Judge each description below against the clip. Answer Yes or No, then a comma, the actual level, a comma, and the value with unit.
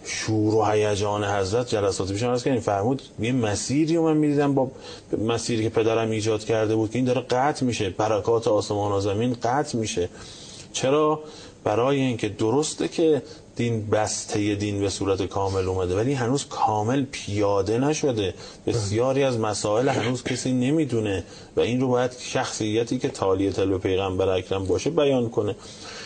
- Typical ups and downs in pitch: Yes, average, 4.2 semitones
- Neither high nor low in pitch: No, low, 115 Hz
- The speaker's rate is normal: No, fast, 160 wpm